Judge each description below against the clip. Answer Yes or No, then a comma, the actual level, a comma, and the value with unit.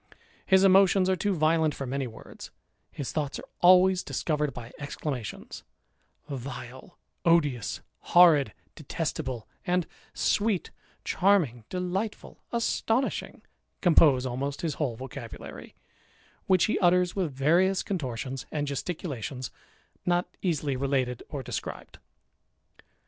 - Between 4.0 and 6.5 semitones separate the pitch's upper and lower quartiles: Yes, wide, 5.4 semitones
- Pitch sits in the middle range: Yes, medium, 150 Hz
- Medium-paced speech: No, slow, 110 wpm